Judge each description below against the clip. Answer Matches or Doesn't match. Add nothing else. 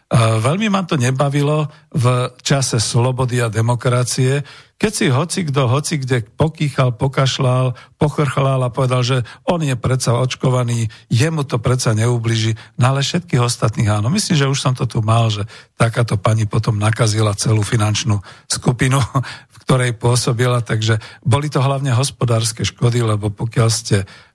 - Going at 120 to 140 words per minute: Doesn't match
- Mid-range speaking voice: Doesn't match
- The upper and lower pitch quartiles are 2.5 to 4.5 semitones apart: Matches